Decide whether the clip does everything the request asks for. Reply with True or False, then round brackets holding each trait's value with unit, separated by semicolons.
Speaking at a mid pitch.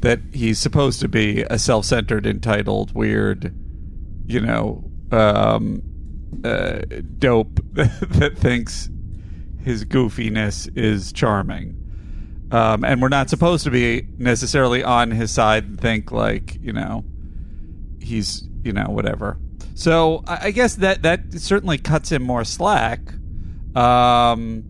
False (110 Hz)